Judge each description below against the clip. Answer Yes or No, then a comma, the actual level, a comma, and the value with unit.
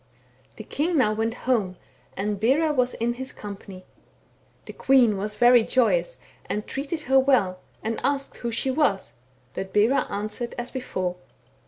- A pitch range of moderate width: Yes, average, 4.3 semitones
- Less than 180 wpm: Yes, average, 160 wpm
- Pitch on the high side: Yes, high, 235 Hz